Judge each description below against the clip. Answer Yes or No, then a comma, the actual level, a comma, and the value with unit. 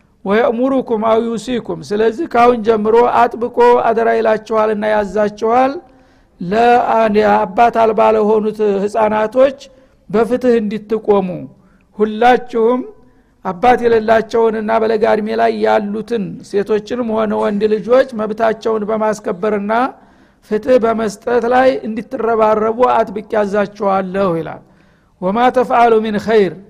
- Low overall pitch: No, high, 225 Hz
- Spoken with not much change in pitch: Yes, narrow, 1.8 semitones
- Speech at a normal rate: Yes, average, 90 wpm